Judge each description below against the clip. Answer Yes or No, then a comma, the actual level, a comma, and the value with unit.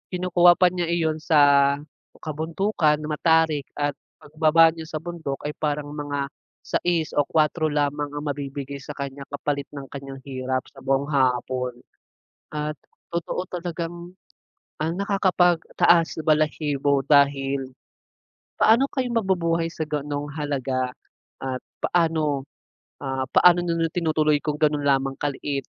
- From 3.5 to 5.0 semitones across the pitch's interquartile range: No, average, 2.9 semitones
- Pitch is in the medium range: Yes, medium, 150 Hz